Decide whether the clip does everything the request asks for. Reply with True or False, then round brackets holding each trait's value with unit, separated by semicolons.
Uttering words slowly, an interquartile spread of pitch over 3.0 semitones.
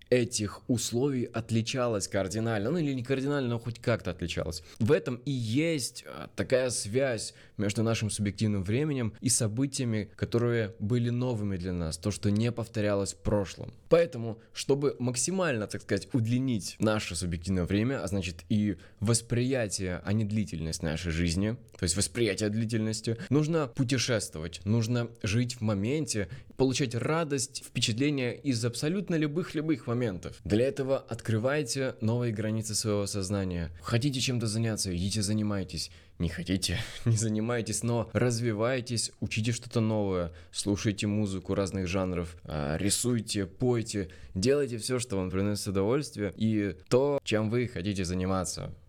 False (135 wpm; 3.7 semitones)